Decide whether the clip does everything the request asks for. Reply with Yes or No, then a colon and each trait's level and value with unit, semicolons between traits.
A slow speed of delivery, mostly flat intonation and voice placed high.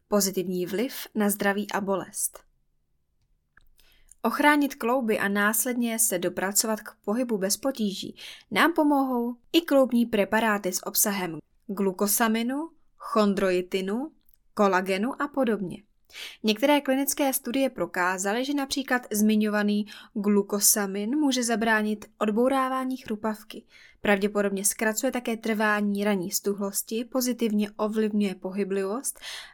No: slow, 100 wpm; average, 4.3 semitones; high, 215 Hz